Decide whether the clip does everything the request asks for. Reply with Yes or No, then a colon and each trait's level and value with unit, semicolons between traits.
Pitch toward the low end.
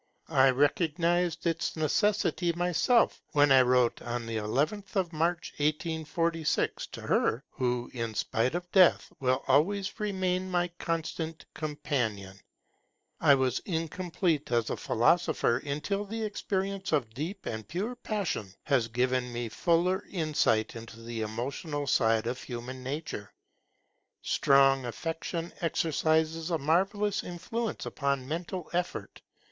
No: medium, 155 Hz